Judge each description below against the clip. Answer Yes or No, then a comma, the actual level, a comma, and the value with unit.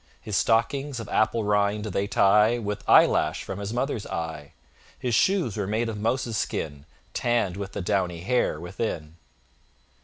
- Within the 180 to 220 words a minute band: No, average, 155 wpm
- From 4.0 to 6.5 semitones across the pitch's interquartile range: No, average, 3.3 semitones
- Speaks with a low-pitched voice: Yes, low, 105 Hz